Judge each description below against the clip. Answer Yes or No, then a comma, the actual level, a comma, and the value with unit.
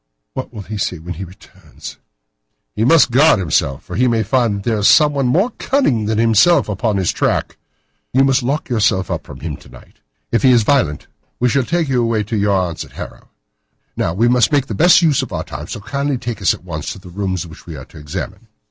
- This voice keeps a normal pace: No, fast, 235 wpm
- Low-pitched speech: Yes, low, 110 Hz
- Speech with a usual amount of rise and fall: No, wide, 5.8 semitones